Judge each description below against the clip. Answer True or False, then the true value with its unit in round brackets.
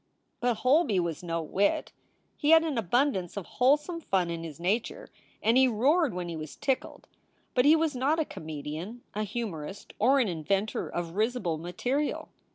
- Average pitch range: False (7.7 semitones)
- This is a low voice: False (215 Hz)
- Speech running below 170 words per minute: False (175 wpm)